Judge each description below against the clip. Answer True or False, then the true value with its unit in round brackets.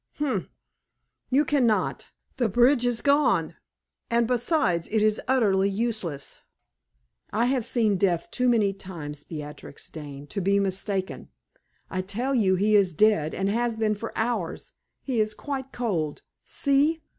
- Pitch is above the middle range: True (215 Hz)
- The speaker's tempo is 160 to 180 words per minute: False (145 wpm)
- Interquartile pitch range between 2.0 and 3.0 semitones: False (4.6 semitones)